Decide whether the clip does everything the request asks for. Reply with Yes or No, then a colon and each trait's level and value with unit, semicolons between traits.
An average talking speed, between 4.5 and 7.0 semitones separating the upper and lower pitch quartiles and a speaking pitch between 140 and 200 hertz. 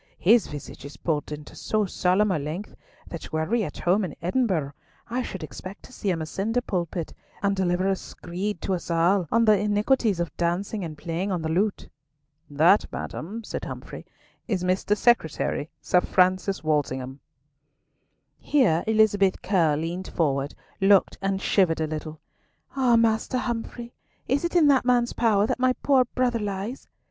Yes: average, 170 wpm; average, 4.9 semitones; high, 190 Hz